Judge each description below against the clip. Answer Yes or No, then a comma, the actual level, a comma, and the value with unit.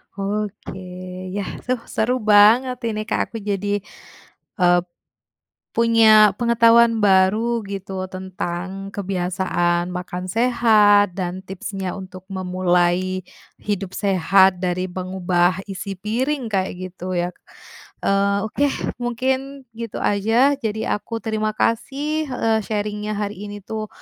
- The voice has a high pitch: Yes, high, 200 Hz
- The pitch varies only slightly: No, average, 3.2 semitones